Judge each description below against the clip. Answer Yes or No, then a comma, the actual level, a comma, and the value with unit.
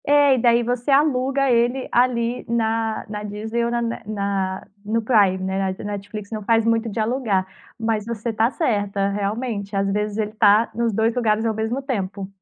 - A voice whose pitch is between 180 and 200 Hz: No, high, 220 Hz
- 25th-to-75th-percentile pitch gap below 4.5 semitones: Yes, narrow, 2.5 semitones